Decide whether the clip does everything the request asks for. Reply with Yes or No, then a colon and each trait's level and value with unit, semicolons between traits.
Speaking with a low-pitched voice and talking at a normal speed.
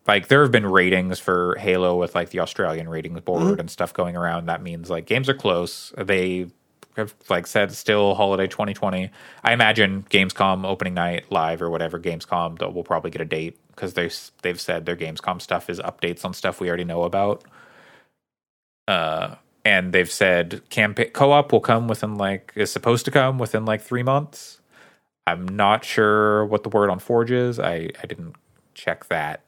Yes: very low, 95 Hz; average, 185 wpm